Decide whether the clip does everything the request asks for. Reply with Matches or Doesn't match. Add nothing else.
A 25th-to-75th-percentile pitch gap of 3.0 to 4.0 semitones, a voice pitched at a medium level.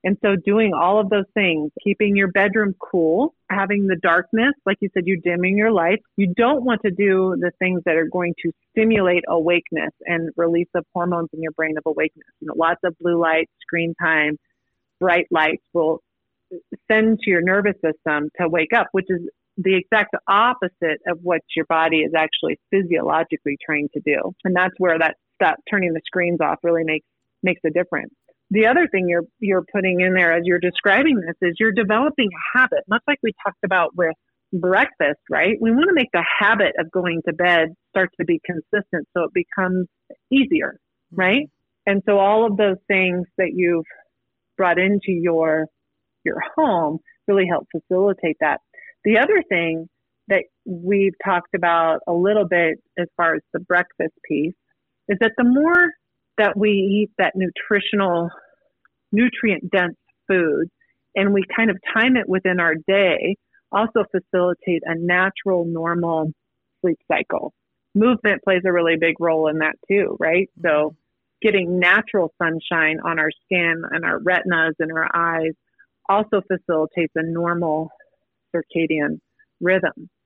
Matches